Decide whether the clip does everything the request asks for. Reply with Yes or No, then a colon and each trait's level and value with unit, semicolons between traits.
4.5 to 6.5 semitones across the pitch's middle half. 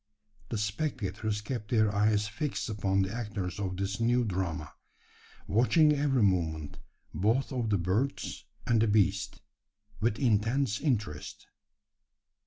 No: average, 3.6 semitones